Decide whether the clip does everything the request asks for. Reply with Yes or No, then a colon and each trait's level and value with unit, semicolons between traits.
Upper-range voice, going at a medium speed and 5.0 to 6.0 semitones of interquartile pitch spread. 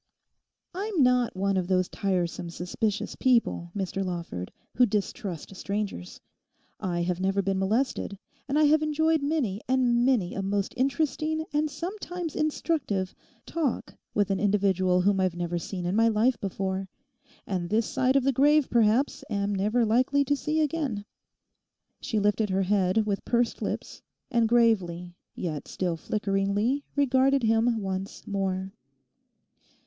Yes: high, 210 Hz; average, 145 wpm; wide, 5.6 semitones